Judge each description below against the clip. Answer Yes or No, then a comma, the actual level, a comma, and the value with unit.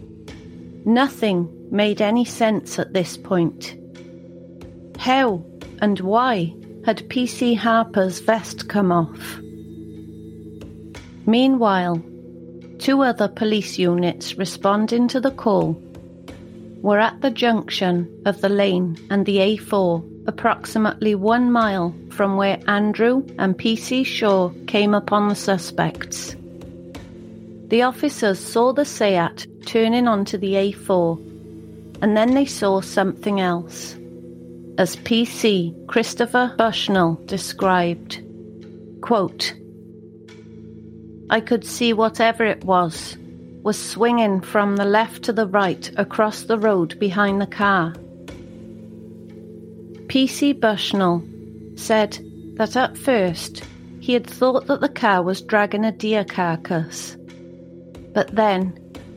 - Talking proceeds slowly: Yes, slow, 110 wpm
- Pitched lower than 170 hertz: No, high, 195 Hz